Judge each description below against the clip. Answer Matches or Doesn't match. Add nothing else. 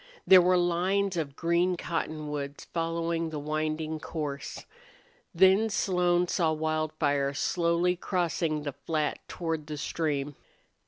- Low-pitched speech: Doesn't match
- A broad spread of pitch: Doesn't match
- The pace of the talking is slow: Matches